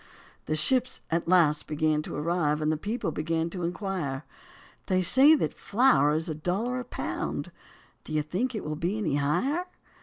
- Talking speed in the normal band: Yes, average, 180 wpm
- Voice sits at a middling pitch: Yes, medium, 170 Hz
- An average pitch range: No, wide, 5.8 semitones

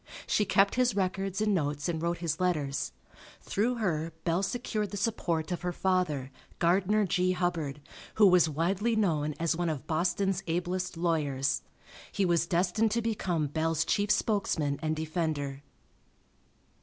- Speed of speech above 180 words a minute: No, average, 150 wpm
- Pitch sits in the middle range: Yes, medium, 175 Hz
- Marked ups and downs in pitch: No, average, 3.7 semitones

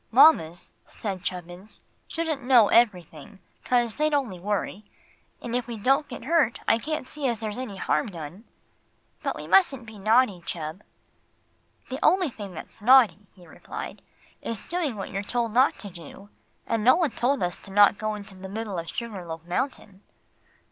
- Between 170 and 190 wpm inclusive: Yes, average, 175 wpm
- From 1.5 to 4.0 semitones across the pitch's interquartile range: No, average, 5.1 semitones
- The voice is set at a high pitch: Yes, high, 215 Hz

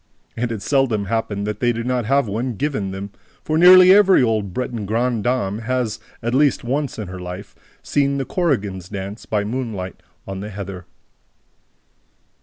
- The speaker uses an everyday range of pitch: Yes, average, 4.5 semitones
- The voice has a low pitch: Yes, low, 115 Hz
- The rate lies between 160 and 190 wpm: Yes, average, 165 wpm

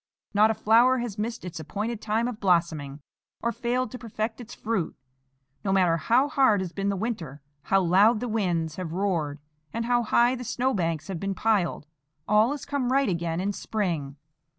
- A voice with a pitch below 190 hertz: No, high, 210 Hz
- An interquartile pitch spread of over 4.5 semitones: Yes, average, 5.2 semitones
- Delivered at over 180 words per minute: Yes, average, 190 wpm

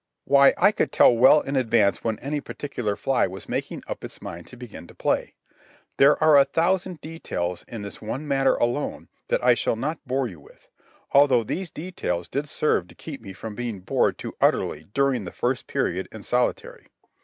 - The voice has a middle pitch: No, low, 125 Hz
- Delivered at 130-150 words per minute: No, average, 195 wpm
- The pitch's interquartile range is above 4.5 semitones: Yes, wide, 5.6 semitones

